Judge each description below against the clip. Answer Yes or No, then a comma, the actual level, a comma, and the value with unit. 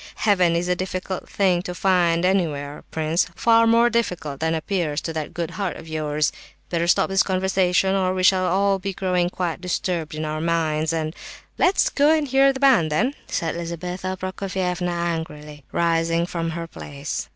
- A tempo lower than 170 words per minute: No, average, 175 wpm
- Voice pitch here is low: No, medium, 175 Hz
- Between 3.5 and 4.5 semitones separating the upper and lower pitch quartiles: No, average, 2.8 semitones